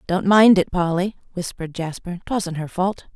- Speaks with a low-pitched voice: No, medium, 180 Hz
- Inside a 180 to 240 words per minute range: No, average, 170 wpm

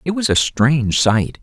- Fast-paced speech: Yes, fast, 210 wpm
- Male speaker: Yes, male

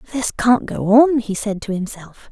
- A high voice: Yes, high, 225 Hz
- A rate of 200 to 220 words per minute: Yes, fast, 205 wpm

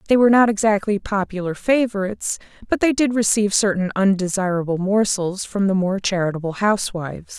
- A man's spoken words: No, female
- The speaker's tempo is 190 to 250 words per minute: No, average, 145 wpm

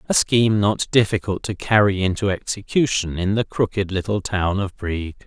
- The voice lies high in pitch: No, low, 100 Hz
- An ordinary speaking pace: Yes, average, 170 wpm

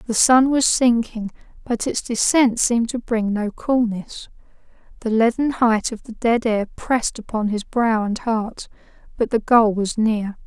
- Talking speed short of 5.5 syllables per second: Yes, 4.3 syllables/s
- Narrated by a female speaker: Yes, female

